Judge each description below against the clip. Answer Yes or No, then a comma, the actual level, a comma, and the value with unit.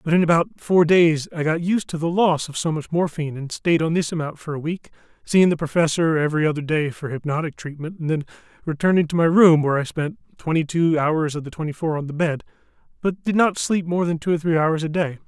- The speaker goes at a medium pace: No, fast, 245 wpm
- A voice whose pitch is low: No, medium, 160 Hz